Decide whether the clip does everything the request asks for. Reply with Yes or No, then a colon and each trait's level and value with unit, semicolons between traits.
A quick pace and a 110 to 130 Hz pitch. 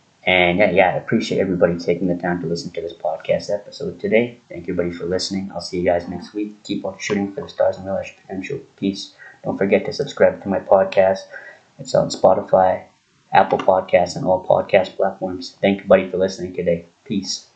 No: fast, 210 wpm; very low, 95 Hz